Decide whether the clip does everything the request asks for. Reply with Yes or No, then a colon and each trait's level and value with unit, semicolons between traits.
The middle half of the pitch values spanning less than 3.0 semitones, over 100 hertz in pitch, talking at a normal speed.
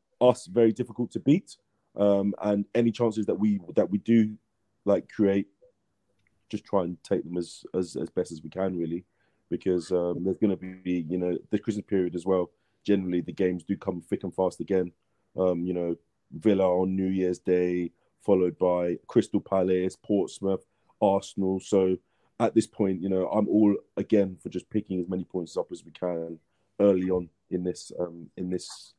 No: narrow, 2.4 semitones; very low, 95 Hz; average, 185 wpm